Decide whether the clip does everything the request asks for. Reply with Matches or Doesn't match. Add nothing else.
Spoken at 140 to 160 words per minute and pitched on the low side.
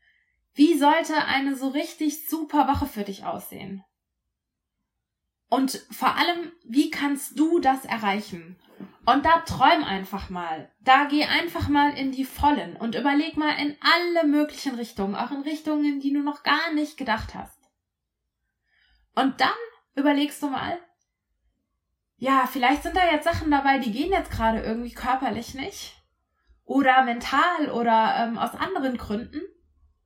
Doesn't match